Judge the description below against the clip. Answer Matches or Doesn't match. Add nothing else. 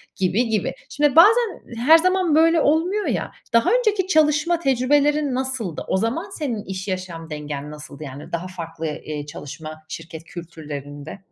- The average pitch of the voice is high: Matches